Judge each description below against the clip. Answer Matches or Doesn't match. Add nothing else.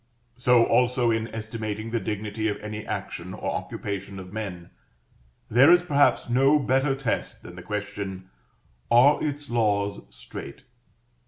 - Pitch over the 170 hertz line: Doesn't match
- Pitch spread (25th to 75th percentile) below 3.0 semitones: Doesn't match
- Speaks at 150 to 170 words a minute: Doesn't match